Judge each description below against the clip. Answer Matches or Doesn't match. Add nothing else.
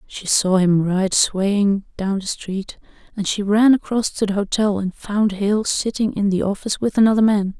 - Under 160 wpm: Doesn't match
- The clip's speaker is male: Doesn't match